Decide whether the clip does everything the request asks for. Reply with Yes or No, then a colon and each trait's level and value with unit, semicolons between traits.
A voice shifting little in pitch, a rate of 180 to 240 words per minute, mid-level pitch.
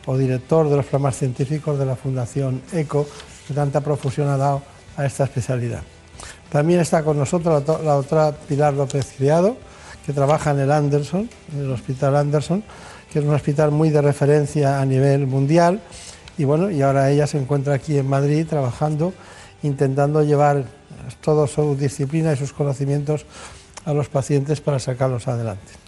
No: narrow, 1.7 semitones; average, 165 wpm; medium, 145 Hz